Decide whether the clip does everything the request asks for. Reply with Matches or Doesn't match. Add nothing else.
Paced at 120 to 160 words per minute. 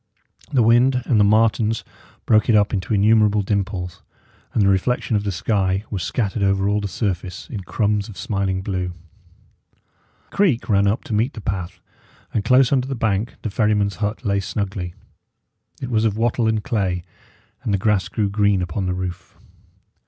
Doesn't match